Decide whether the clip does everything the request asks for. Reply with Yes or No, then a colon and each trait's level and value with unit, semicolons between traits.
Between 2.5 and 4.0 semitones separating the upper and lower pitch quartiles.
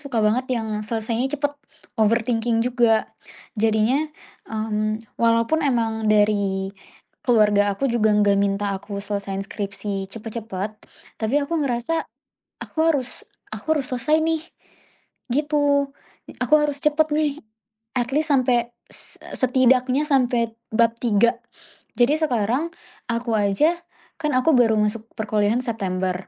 No: average, 4.5 semitones